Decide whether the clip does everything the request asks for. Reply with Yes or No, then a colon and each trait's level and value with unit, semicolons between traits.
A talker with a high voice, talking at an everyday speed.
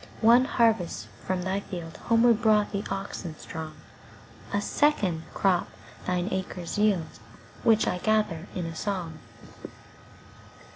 No: high, 195 Hz; slow, 105 wpm